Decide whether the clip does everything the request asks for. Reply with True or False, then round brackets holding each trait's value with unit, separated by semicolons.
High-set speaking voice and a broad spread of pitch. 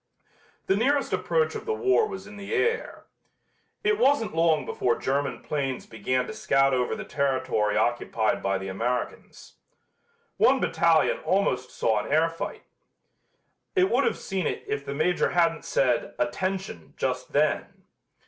False (155 Hz; 8.7 semitones)